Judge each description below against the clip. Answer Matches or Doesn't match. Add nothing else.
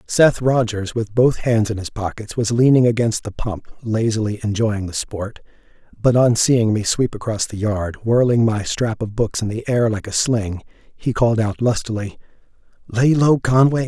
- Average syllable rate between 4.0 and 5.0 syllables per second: Matches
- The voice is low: Matches